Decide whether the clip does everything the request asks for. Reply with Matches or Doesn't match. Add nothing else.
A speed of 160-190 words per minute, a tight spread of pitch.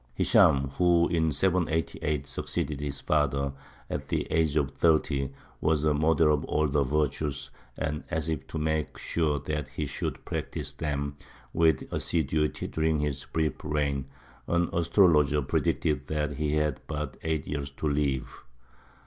Doesn't match